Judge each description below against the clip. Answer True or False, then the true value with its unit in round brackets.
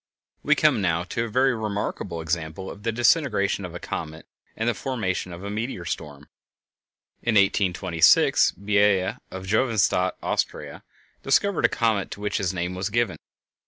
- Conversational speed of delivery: True (160 wpm)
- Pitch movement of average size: True (3.8 semitones)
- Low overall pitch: True (100 Hz)